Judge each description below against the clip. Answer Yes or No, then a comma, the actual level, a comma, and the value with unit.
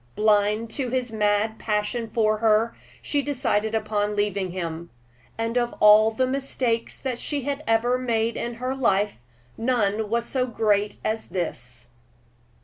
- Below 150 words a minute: Yes, average, 140 wpm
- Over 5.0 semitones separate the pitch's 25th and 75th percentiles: No, average, 2.7 semitones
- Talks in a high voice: Yes, high, 220 Hz